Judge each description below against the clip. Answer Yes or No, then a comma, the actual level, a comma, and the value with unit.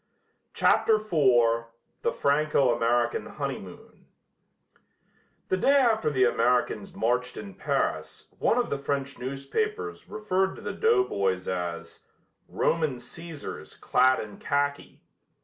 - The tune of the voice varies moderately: No, wide, 7.7 semitones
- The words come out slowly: Yes, slow, 115 wpm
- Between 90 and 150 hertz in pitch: Yes, medium, 140 Hz